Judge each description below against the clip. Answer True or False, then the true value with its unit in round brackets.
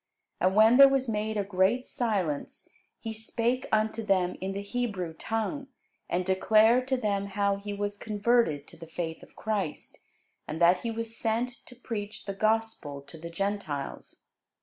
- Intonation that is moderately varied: True (3.3 semitones)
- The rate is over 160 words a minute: True (170 wpm)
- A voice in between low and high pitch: False (210 Hz)